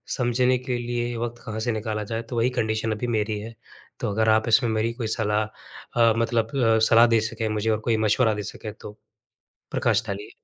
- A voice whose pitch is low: Yes, low, 115 Hz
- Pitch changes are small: Yes, narrow, 1.6 semitones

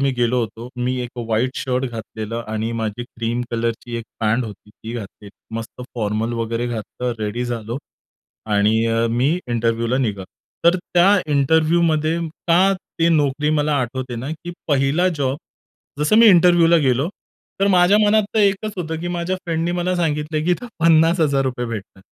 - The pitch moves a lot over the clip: Yes, wide, 6.2 semitones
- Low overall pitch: Yes, low, 130 Hz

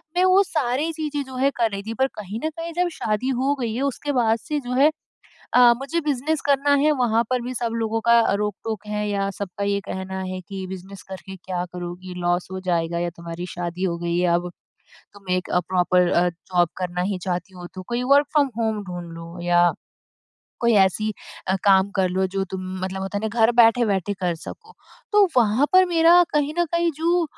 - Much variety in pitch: Yes, wide, 6.4 semitones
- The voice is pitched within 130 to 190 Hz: No, high, 210 Hz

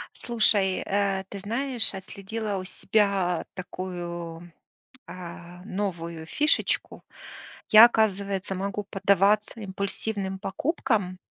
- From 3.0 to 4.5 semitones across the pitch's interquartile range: No, narrow, 2.4 semitones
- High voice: Yes, high, 195 Hz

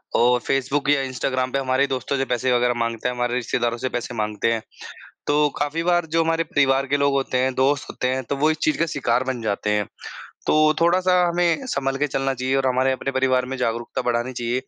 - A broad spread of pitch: No, narrow, 2.6 semitones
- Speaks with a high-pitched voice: No, low, 130 Hz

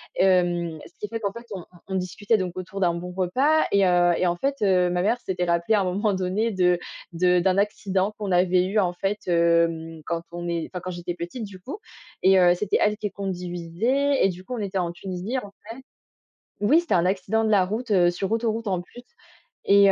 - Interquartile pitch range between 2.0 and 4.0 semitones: Yes, average, 2.9 semitones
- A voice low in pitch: No, medium, 185 Hz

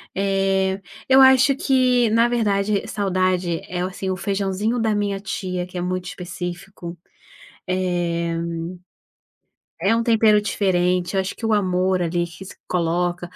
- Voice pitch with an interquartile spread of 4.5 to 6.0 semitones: No, average, 2.8 semitones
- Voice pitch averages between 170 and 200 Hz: Yes, high, 190 Hz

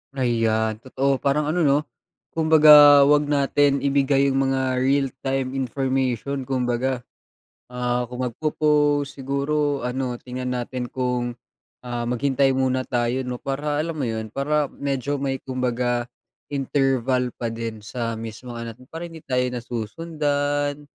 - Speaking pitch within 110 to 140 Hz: Yes, low, 135 Hz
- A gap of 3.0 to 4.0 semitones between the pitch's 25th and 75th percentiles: No, narrow, 2.5 semitones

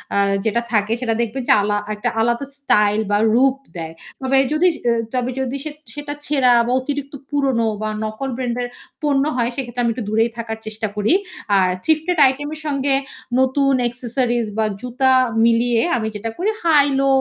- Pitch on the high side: Yes, high, 245 Hz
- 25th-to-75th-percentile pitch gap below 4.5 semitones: Yes, average, 3.5 semitones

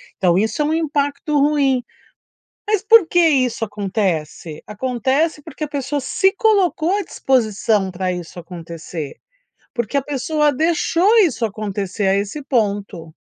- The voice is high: Yes, very high, 255 Hz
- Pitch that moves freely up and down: Yes, wide, 7.4 semitones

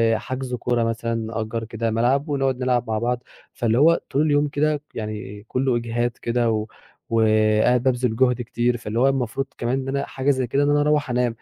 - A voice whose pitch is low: Yes, low, 120 Hz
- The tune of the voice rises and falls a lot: No, average, 2.9 semitones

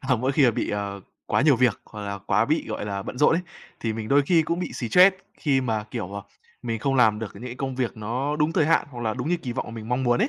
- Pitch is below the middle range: Yes, low, 125 Hz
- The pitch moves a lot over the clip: No, average, 4.7 semitones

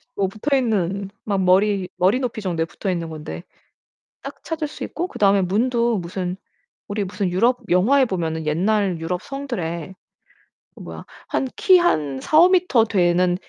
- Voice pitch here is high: Yes, high, 195 Hz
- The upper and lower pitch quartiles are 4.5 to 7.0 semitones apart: Yes, average, 5.2 semitones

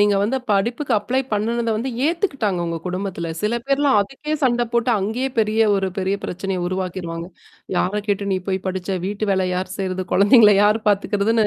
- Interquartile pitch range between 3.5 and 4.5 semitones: Yes, average, 3.8 semitones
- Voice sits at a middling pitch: No, high, 205 Hz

